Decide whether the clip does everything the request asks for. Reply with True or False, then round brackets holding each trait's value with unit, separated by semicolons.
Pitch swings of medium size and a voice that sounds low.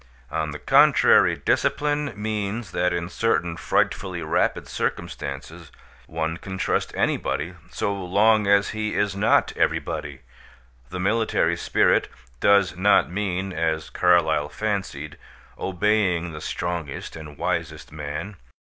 True (4.0 semitones; 90 Hz)